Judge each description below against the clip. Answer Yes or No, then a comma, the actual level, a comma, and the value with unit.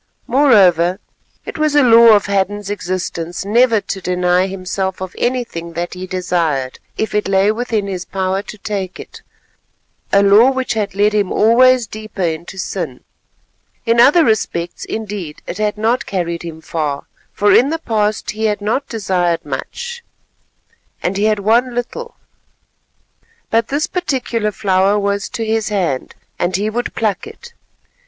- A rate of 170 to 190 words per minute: No, average, 155 wpm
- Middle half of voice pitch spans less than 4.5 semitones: Yes, average, 3.8 semitones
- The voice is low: No, high, 205 Hz